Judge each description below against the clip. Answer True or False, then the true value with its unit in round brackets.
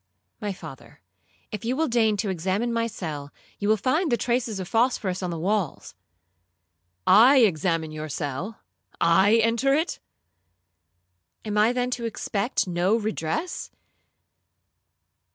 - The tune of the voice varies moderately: False (8.4 semitones)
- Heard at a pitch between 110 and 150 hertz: False (190 Hz)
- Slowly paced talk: True (125 wpm)